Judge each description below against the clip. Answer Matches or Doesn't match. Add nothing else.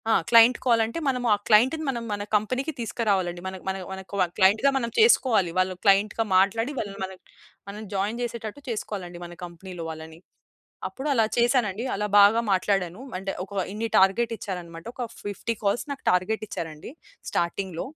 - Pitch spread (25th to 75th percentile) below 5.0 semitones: Matches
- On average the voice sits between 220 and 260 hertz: Doesn't match